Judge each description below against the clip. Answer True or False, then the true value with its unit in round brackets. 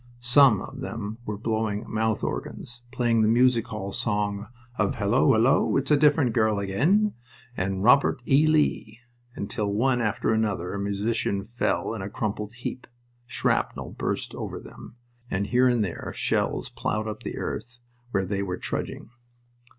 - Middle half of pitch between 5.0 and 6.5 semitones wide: False (3.2 semitones)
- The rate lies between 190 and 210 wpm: False (160 wpm)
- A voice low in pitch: True (110 Hz)